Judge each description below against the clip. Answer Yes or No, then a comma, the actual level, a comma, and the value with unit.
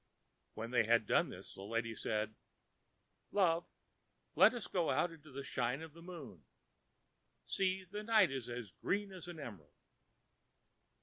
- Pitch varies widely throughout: Yes, wide, 7.9 semitones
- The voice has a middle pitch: Yes, medium, 145 Hz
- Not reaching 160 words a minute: Yes, average, 150 wpm